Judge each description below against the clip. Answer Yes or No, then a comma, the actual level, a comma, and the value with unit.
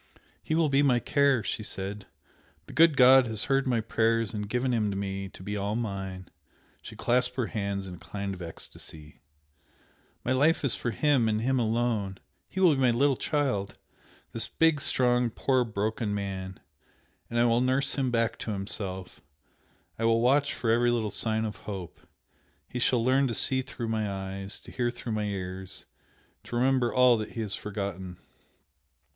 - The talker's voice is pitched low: Yes, low, 115 Hz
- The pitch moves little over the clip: No, average, 4.2 semitones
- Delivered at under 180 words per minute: No, average, 185 wpm